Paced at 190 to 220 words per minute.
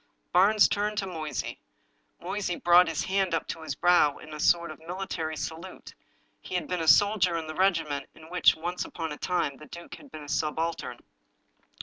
Yes: average, 200 wpm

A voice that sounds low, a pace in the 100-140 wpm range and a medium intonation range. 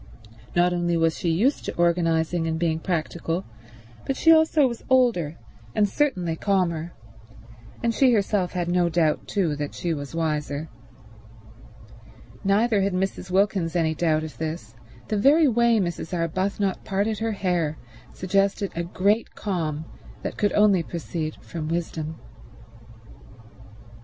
No: medium, 175 Hz; slow, 135 wpm; average, 3.8 semitones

